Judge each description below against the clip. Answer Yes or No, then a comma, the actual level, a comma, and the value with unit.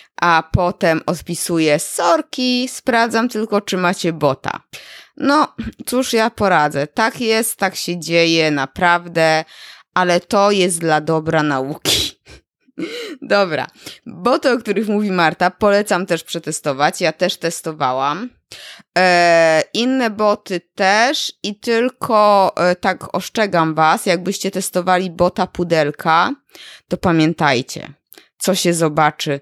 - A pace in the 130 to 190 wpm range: No, average, 115 wpm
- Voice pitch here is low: No, medium, 180 Hz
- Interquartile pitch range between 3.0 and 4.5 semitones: No, average, 5.2 semitones